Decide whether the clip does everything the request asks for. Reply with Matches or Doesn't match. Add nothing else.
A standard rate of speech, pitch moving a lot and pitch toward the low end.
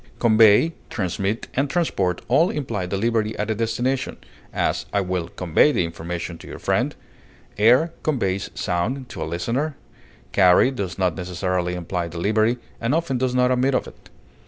Matches